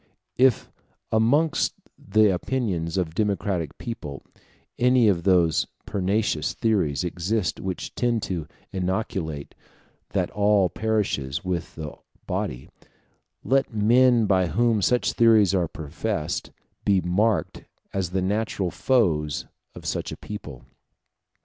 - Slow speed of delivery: Yes, slow, 120 wpm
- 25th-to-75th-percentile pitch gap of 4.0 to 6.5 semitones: Yes, average, 4.7 semitones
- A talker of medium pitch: No, very low, 95 Hz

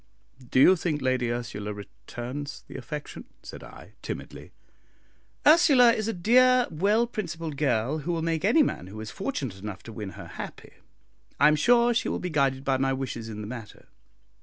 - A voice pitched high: No, medium, 145 Hz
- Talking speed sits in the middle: Yes, average, 185 wpm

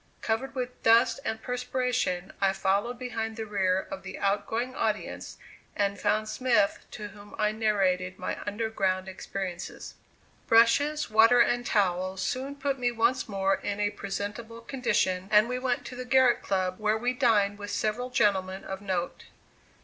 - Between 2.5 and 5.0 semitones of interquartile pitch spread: Yes, average, 3.9 semitones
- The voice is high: Yes, high, 215 Hz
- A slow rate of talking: No, average, 160 wpm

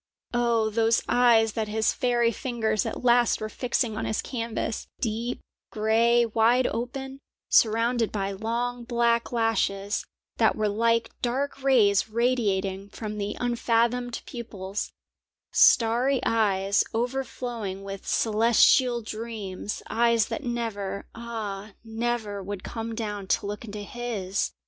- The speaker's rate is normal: No, slow, 125 wpm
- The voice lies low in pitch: No, high, 230 Hz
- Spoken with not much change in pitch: Yes, narrow, 2.2 semitones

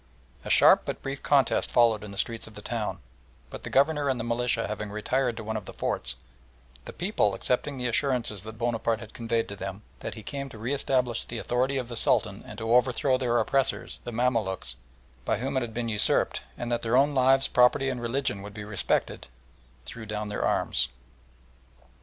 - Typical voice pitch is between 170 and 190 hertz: No, low, 120 Hz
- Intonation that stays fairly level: No, average, 3.0 semitones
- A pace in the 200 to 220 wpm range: Yes, fast, 205 wpm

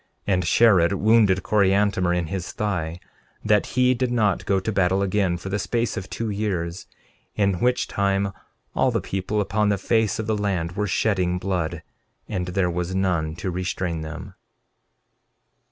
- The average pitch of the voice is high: No, very low, 95 Hz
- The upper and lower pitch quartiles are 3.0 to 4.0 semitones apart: No, narrow, 2.6 semitones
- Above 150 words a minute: Yes, average, 170 wpm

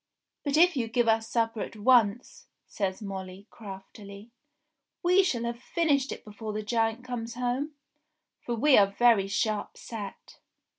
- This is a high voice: Yes, high, 230 Hz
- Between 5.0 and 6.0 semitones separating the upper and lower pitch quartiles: No, average, 3.2 semitones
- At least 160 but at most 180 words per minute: No, average, 150 wpm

